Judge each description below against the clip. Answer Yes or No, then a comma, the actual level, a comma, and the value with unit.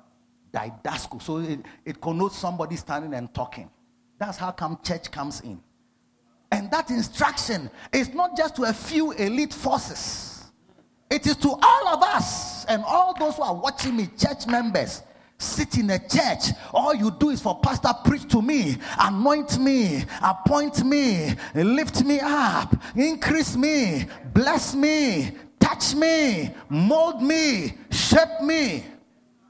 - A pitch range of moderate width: No, wide, 7.7 semitones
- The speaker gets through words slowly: No, average, 145 wpm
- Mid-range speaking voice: No, very high, 250 Hz